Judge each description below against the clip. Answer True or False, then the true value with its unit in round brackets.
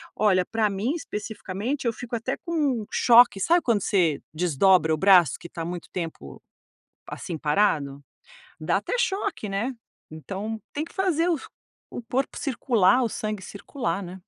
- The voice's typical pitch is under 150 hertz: False (210 Hz)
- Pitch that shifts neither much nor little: False (5.8 semitones)